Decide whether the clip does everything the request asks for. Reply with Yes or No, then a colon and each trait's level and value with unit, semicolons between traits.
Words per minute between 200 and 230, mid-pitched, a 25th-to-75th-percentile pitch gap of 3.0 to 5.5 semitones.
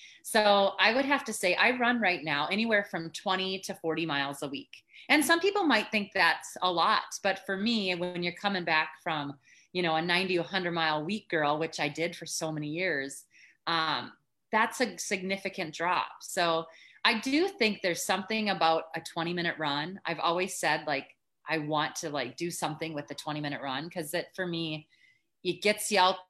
Yes: fast, 205 wpm; medium, 180 Hz; average, 4.3 semitones